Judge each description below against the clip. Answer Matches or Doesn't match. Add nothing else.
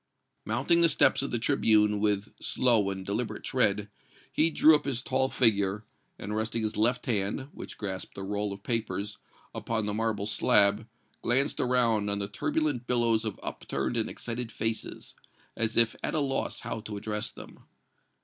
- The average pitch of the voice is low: Matches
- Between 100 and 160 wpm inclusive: Doesn't match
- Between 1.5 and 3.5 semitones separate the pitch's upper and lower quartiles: Matches